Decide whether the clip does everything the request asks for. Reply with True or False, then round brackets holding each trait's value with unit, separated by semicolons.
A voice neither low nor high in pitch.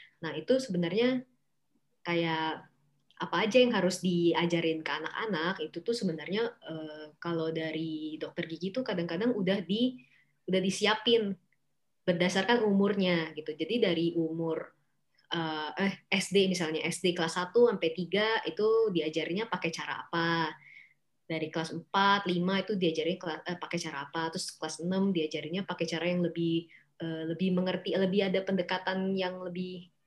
True (175 Hz)